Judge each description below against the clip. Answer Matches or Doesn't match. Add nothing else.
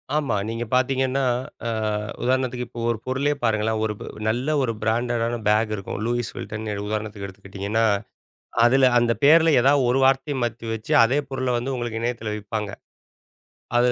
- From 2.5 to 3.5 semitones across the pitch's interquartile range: Matches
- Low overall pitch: Matches